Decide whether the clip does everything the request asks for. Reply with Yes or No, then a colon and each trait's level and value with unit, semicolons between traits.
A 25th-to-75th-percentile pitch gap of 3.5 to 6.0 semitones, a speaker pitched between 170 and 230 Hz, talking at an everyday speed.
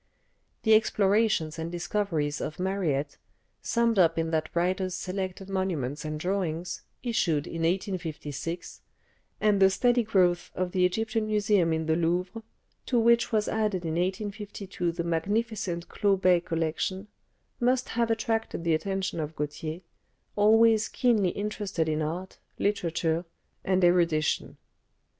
No: average, 4.1 semitones; medium, 185 Hz; slow, 130 wpm